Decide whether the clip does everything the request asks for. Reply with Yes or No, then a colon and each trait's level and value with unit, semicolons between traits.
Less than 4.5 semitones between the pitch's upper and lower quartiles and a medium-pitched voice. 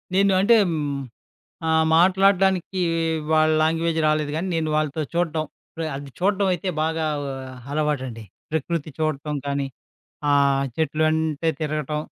Yes: narrow, 2.5 semitones; medium, 160 Hz